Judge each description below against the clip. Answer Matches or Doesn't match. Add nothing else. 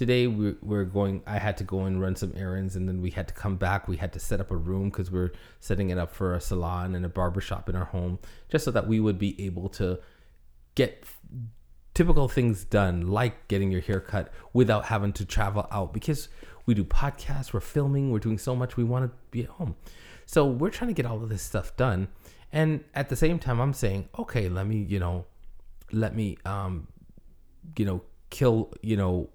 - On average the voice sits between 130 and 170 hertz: Doesn't match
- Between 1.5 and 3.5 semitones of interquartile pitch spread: Doesn't match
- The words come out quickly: Matches